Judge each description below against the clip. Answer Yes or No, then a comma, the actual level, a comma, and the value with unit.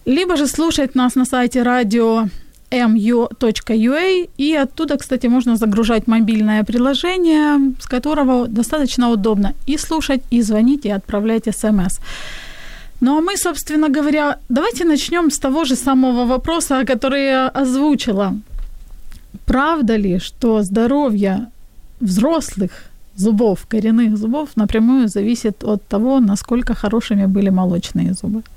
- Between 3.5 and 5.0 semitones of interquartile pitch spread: Yes, average, 4.1 semitones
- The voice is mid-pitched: No, high, 245 Hz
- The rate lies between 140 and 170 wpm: No, average, 120 wpm